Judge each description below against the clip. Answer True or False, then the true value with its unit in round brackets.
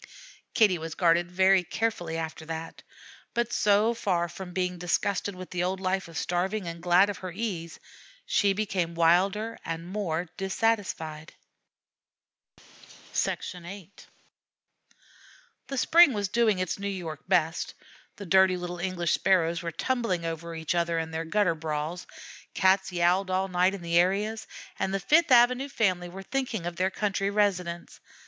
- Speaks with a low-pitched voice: False (185 Hz)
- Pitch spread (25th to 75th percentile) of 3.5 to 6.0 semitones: False (3.0 semitones)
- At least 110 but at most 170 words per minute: True (150 wpm)